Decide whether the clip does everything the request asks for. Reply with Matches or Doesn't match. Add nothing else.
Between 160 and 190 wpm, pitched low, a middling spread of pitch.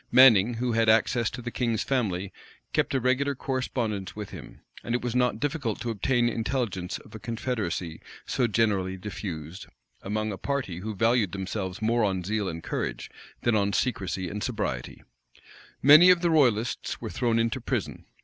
Matches